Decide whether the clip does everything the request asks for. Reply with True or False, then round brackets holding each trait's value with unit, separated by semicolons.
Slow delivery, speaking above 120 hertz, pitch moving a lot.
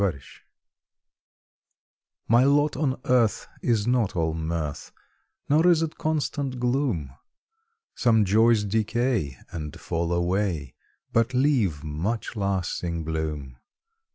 False (110 wpm; 105 Hz; 7.5 semitones)